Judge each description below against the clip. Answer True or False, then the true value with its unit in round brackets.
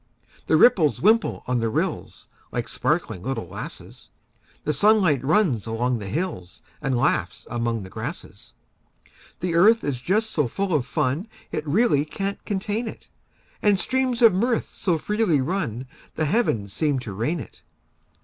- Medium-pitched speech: True (155 Hz)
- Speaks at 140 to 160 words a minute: True (155 wpm)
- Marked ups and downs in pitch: True (8.7 semitones)